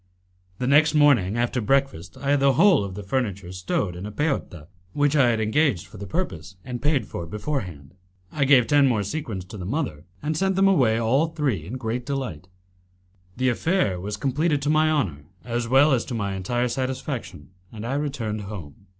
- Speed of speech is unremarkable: Yes, average, 195 wpm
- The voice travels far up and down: Yes, wide, 6.4 semitones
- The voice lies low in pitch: Yes, low, 120 Hz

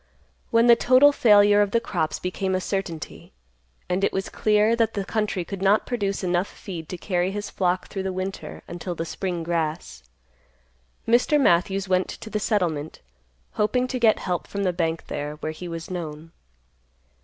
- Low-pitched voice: No, high, 190 Hz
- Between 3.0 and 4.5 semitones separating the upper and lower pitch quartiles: Yes, average, 3.3 semitones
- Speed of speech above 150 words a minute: Yes, average, 180 wpm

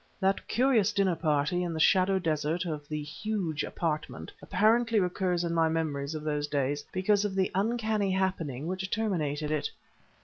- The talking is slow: No, average, 165 wpm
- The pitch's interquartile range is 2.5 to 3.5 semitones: No, average, 4.4 semitones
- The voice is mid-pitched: Yes, medium, 175 Hz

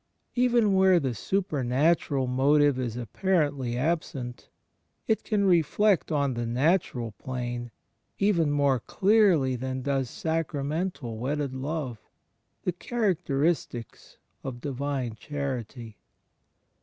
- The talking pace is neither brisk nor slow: No, slow, 100 wpm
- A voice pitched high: No, medium, 140 Hz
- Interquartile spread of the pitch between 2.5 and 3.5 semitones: No, wide, 5.4 semitones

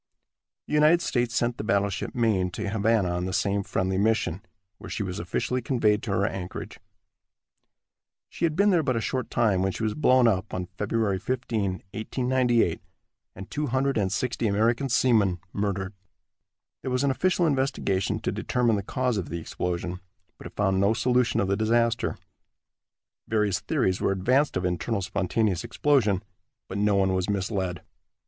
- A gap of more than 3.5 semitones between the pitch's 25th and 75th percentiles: Yes, average, 4.5 semitones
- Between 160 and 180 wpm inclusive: Yes, average, 165 wpm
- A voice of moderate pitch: No, low, 105 Hz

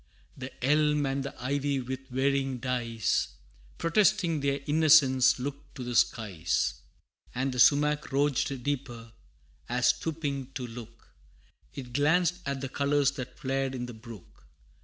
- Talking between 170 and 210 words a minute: No, slow, 135 wpm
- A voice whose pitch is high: No, low, 135 Hz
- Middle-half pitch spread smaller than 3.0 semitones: Yes, narrow, 2.6 semitones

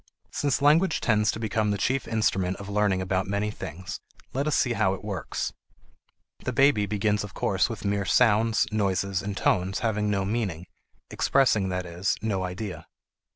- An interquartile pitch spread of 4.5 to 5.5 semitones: No, average, 2.7 semitones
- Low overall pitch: Yes, low, 105 Hz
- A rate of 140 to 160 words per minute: No, average, 170 wpm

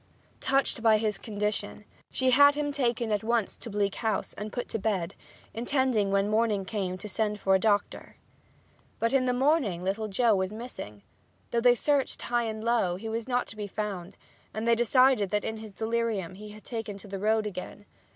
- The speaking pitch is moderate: No, high, 220 Hz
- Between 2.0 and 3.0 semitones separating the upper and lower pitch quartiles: Yes, average, 2.7 semitones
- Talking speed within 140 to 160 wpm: No, average, 200 wpm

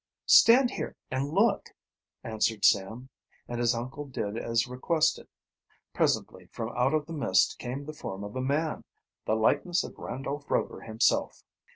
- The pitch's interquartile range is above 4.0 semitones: Yes, average, 4.6 semitones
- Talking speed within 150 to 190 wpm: Yes, average, 155 wpm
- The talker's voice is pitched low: Yes, low, 130 Hz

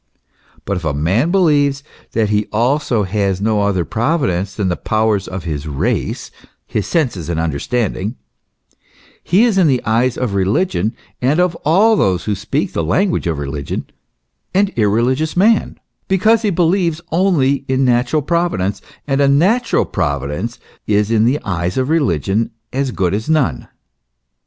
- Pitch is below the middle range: Yes, low, 115 Hz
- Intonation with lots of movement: Yes, wide, 8.4 semitones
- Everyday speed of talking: Yes, average, 160 wpm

